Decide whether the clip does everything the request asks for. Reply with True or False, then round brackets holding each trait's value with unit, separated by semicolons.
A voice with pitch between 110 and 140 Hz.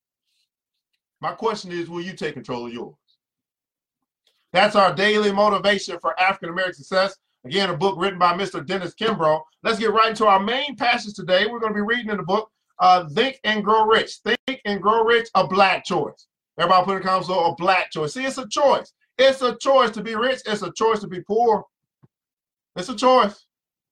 False (205 Hz)